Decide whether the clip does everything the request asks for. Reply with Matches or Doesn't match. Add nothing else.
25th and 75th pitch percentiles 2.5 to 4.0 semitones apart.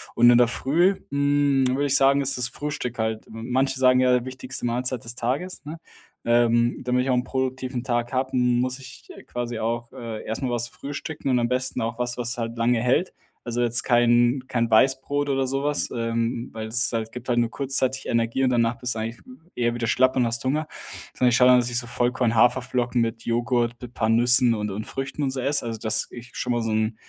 Doesn't match